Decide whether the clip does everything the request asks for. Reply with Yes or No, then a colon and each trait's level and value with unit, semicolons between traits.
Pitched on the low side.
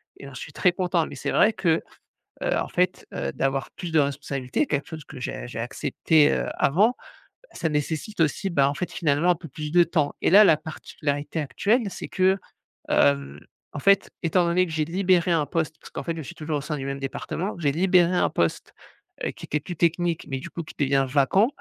No: medium, 160 Hz